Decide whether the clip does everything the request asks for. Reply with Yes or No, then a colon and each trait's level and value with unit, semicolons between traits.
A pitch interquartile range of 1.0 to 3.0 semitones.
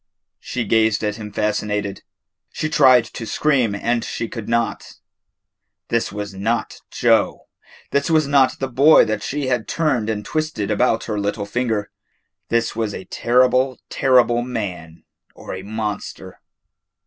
No: average, 3.6 semitones